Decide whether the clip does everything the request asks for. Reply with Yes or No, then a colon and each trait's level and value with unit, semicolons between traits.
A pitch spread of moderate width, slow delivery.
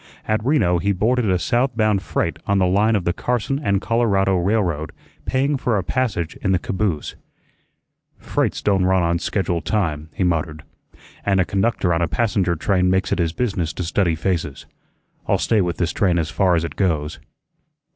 No: average, 3.9 semitones; average, 185 wpm